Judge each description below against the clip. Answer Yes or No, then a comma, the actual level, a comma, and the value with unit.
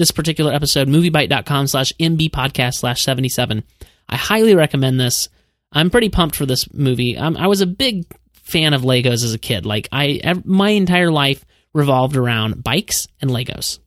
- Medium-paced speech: Yes, average, 175 wpm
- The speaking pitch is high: No, medium, 140 Hz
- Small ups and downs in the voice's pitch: No, average, 4.7 semitones